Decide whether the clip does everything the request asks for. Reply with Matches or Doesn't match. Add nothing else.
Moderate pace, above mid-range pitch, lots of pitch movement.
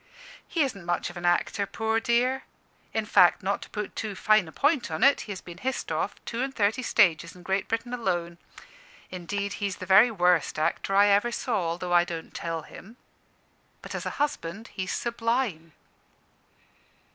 Doesn't match